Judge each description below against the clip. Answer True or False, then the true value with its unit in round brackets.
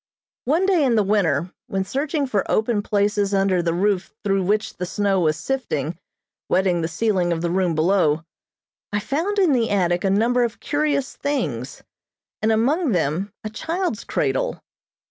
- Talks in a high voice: True (205 Hz)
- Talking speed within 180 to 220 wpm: False (165 wpm)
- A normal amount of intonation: False (6.4 semitones)